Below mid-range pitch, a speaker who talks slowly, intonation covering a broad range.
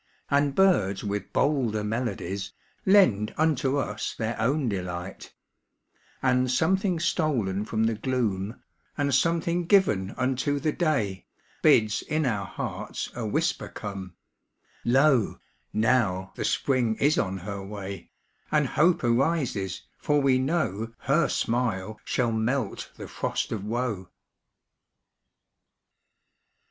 Yes: low, 120 Hz; slow, 125 wpm; wide, 5.9 semitones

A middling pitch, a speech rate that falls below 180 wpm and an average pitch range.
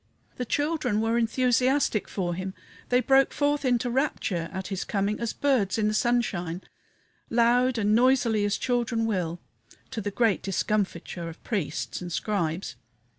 No: high, 220 Hz; average, 150 wpm; average, 4.5 semitones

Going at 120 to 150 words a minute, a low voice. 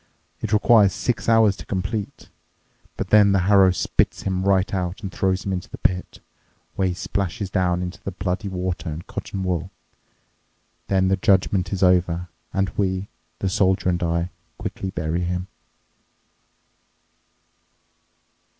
Yes: average, 145 wpm; very low, 95 Hz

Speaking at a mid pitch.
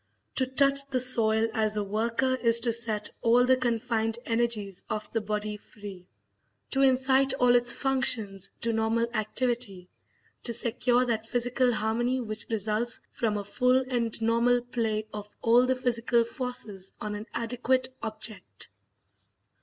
No: high, 230 Hz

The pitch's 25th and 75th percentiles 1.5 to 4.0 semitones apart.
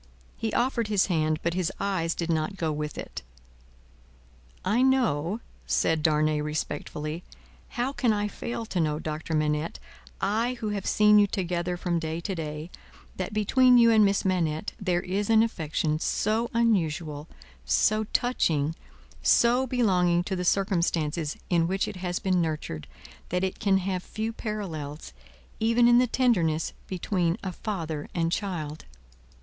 No: average, 5.1 semitones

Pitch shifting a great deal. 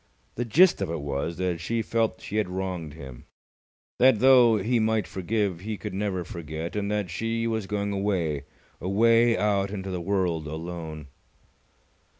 No: average, 4.6 semitones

